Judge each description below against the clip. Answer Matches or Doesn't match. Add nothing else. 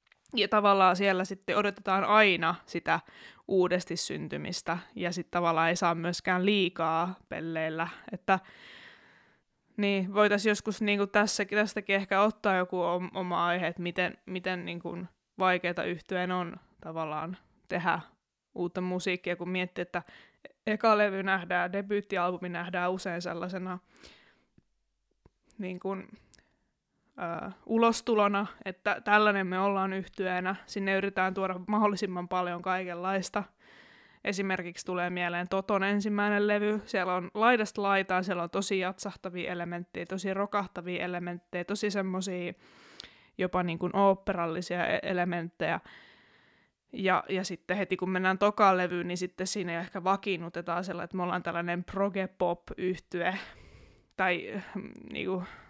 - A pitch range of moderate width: Doesn't match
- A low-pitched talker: Doesn't match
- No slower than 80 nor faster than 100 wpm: Doesn't match